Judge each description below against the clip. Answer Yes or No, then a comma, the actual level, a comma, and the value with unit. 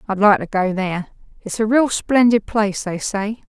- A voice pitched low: No, high, 210 Hz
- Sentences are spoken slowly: No, fast, 205 wpm